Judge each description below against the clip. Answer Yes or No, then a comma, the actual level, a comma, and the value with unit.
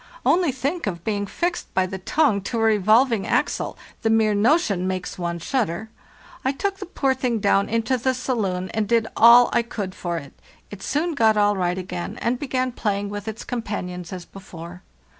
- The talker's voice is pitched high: Yes, high, 215 Hz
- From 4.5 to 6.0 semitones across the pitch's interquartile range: Yes, average, 5.2 semitones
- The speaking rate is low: No, average, 185 wpm